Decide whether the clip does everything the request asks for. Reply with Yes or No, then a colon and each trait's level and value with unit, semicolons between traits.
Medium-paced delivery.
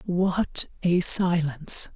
No: slow, 90 wpm